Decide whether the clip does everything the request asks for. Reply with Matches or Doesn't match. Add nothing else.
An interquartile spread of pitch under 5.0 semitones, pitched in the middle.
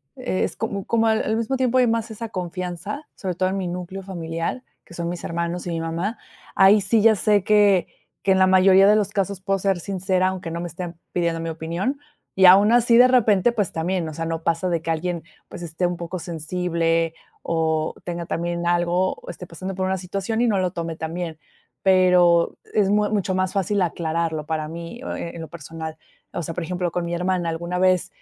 Matches